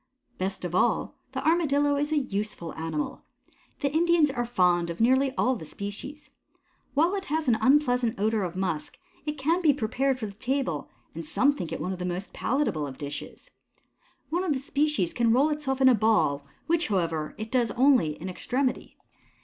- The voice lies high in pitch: Yes, high, 240 Hz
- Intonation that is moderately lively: No, wide, 7.9 semitones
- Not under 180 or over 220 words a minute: Yes, average, 190 wpm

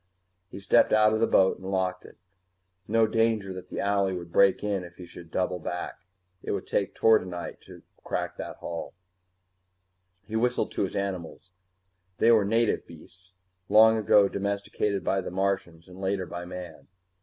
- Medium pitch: No, very low, 95 Hz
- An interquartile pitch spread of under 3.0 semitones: Yes, narrow, 2.5 semitones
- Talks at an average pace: Yes, average, 170 wpm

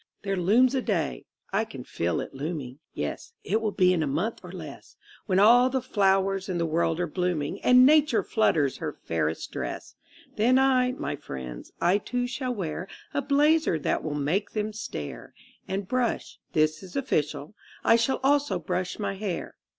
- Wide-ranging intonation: Yes, wide, 7.8 semitones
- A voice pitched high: Yes, high, 195 Hz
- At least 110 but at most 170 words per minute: No, average, 180 wpm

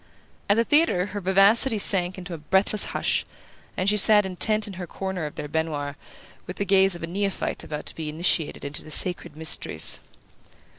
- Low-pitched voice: No, medium, 185 Hz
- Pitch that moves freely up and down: No, average, 3.9 semitones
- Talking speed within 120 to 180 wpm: No, average, 190 wpm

